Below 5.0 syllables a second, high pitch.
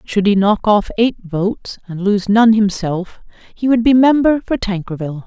Yes: 4.6 syllables/s; high, 210 Hz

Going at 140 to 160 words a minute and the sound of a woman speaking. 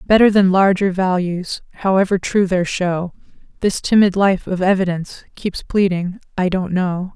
Yes: average, 150 wpm; female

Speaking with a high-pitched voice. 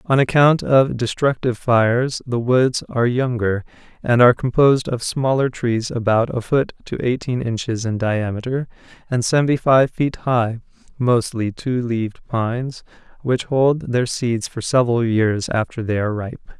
No: low, 120 Hz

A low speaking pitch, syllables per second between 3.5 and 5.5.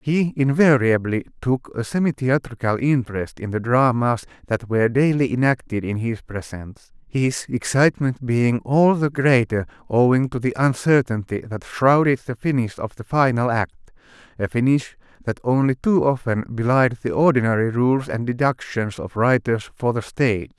Yes: low, 125 Hz; 4.8 syllables/s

